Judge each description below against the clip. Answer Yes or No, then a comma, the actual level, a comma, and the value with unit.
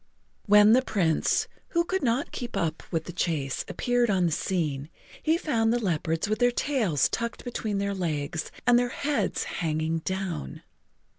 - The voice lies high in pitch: Yes, high, 200 Hz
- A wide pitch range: Yes, wide, 6.9 semitones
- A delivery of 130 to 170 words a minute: Yes, average, 165 wpm